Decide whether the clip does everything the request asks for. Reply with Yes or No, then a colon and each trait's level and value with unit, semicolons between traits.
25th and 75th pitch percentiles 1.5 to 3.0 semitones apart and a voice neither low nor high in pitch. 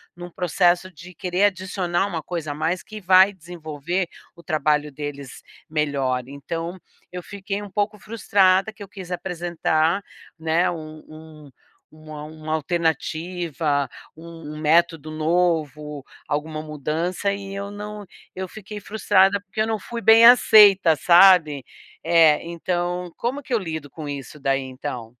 No: average, 3.7 semitones; medium, 170 Hz